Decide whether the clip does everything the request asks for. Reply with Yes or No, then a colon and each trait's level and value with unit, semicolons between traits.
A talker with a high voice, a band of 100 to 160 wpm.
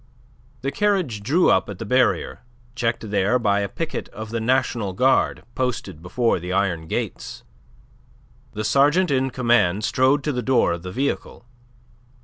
No: low, 120 Hz; average, 155 wpm